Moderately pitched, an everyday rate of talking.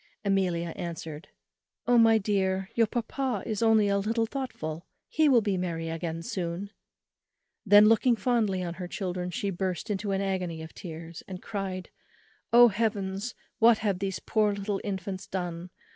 No: high, 195 Hz; average, 160 wpm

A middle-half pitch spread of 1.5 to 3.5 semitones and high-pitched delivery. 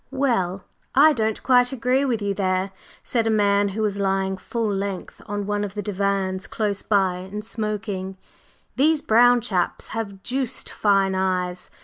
Yes: average, 2.8 semitones; high, 205 Hz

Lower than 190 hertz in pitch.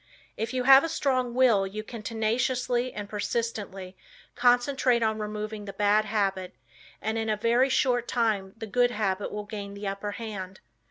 No: high, 220 Hz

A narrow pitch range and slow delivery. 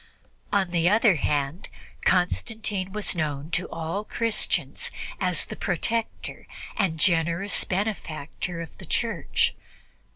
No: average, 4.0 semitones; slow, 110 wpm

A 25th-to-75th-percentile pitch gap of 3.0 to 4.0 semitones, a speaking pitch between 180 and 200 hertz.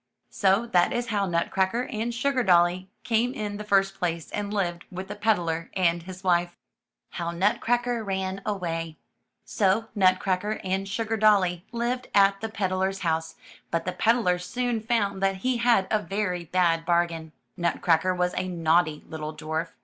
Yes: average, 3.6 semitones; high, 190 Hz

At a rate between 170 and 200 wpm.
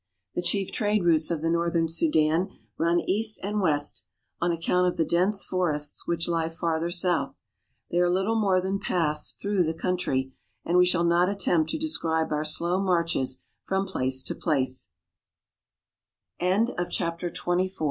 No: average, 145 wpm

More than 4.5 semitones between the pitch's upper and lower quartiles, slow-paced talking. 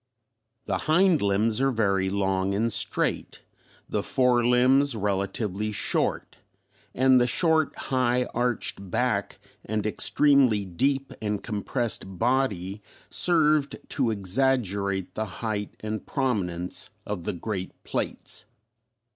Yes: average, 4.9 semitones; slow, 115 wpm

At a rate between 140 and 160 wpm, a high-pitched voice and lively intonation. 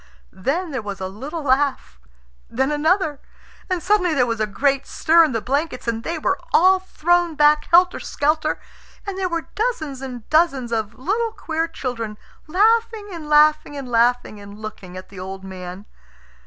No: average, 170 wpm; very high, 290 Hz; wide, 6.7 semitones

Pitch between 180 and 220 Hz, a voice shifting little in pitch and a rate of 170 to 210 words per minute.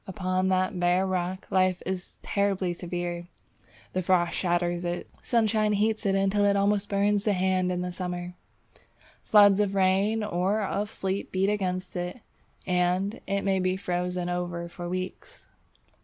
No: medium, 185 Hz; narrow, 1.9 semitones; average, 150 wpm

